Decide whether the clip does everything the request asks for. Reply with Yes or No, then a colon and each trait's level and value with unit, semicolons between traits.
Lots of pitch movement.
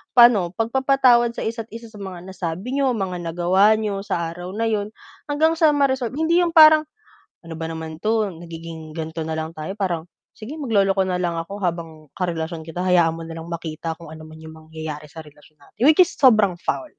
Yes: wide, 6.0 semitones